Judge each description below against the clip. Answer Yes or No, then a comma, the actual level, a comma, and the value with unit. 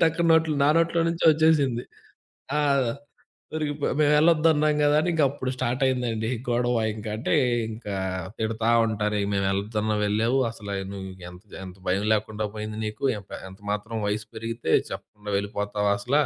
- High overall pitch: No, low, 115 Hz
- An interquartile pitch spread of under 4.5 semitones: No, wide, 5.8 semitones